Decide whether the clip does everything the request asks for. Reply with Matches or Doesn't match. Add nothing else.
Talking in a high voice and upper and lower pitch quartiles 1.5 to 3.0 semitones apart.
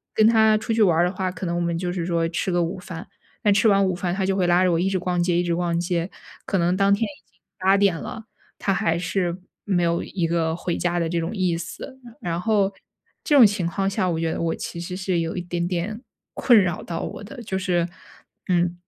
Doesn't match